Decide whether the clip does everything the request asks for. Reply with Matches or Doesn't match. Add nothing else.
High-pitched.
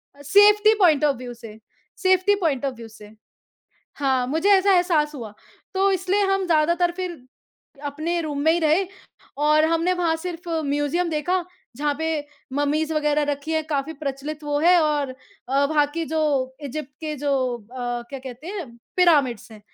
Matches